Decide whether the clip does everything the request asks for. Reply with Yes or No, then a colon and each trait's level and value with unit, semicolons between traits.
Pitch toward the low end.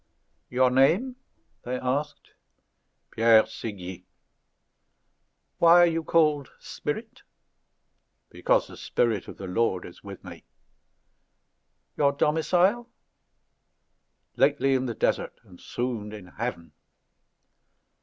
Yes: low, 125 Hz